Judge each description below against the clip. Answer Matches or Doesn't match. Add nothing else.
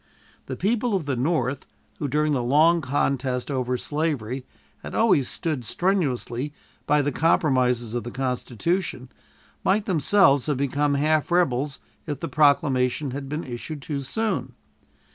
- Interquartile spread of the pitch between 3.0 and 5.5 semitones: Matches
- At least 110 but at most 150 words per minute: Matches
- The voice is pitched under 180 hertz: Matches